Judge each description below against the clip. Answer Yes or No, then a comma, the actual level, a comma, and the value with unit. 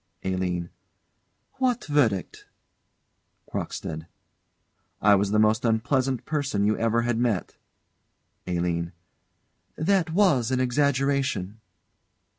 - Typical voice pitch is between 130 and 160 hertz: No, low, 115 Hz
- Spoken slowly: Yes, slow, 90 wpm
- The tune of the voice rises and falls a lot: Yes, wide, 6.1 semitones